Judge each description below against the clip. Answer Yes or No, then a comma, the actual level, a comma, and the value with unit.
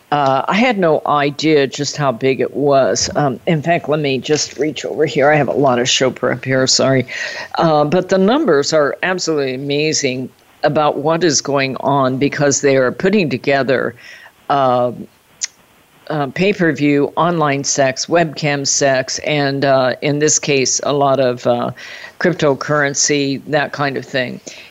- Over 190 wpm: No, average, 165 wpm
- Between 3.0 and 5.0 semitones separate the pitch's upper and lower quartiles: No, narrow, 2.4 semitones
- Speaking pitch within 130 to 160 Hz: Yes, medium, 140 Hz